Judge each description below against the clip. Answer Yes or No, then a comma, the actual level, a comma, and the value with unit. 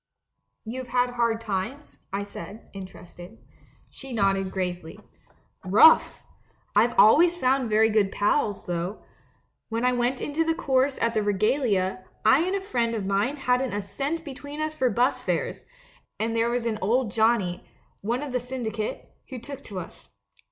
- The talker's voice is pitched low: No, high, 230 Hz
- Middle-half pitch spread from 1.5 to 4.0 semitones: No, average, 4.4 semitones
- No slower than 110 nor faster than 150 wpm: No, average, 170 wpm